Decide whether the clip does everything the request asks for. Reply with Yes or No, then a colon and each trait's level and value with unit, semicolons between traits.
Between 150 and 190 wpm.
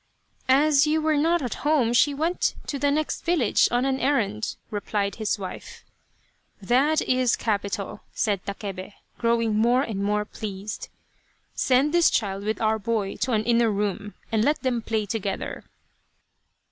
Yes: average, 170 wpm